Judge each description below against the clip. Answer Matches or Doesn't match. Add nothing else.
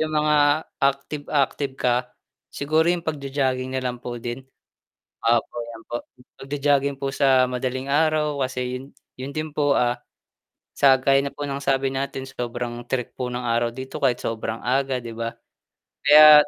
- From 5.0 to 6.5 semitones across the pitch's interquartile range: Doesn't match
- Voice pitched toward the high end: Doesn't match